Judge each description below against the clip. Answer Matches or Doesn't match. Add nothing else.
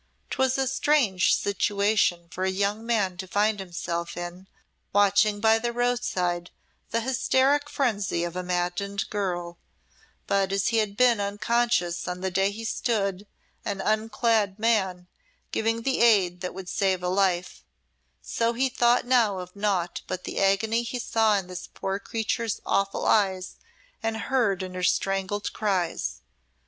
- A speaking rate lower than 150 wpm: Doesn't match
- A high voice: Matches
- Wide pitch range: Doesn't match